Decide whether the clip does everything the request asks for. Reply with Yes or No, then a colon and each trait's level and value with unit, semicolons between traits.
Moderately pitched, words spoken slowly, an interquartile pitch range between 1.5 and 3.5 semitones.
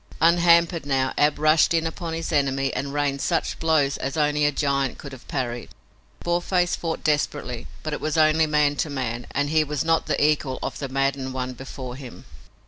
No: medium, 145 Hz; average, 195 wpm; average, 2.9 semitones